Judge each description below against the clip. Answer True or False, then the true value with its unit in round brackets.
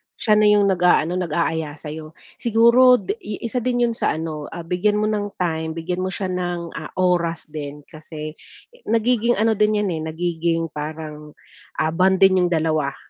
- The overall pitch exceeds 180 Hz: False (175 Hz)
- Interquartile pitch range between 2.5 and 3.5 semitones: False (4.7 semitones)